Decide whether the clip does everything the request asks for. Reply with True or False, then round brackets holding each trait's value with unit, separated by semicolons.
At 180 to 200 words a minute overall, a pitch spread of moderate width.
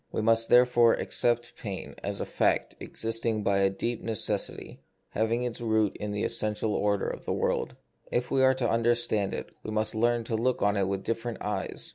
False (195 wpm; 2.2 semitones)